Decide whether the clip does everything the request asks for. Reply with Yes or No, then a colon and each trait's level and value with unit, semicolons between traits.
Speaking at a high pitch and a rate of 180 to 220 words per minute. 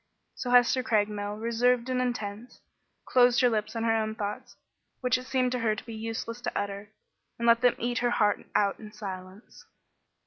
Yes: high, 230 Hz; average, 185 wpm